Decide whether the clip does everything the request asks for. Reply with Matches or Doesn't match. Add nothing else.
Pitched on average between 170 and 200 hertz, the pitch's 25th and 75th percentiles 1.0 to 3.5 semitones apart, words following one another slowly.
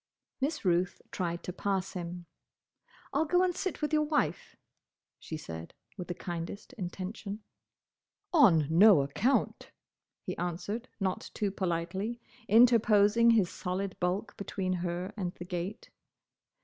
Doesn't match